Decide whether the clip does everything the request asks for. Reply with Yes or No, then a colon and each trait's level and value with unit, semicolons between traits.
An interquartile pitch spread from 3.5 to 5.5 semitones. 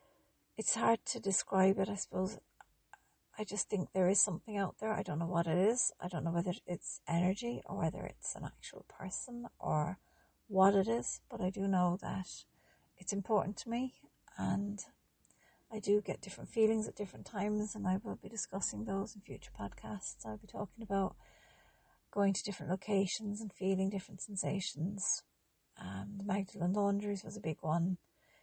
No: narrow, 2.4 semitones